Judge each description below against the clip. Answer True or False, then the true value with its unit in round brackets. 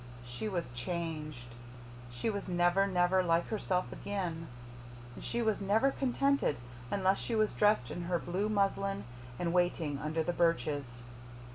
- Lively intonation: False (3.8 semitones)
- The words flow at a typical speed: True (145 wpm)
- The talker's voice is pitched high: False (175 Hz)